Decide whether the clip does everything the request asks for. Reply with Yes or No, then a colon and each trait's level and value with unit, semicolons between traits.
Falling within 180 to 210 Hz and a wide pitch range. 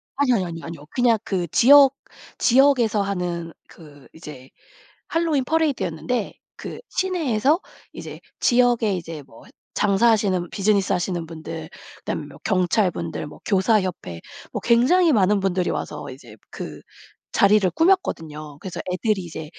Yes: high, 195 Hz; wide, 6.6 semitones